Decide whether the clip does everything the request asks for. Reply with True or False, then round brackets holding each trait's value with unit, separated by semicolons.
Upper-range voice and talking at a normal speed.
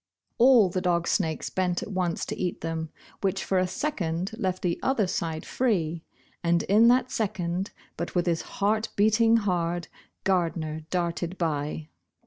False (180 Hz; 155 wpm)